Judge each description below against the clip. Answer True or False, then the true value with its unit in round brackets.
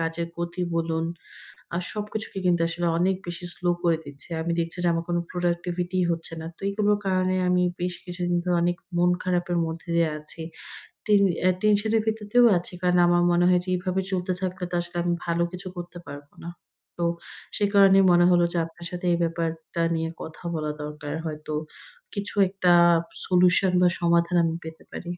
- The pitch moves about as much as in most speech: False (1.6 semitones)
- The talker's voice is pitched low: False (175 Hz)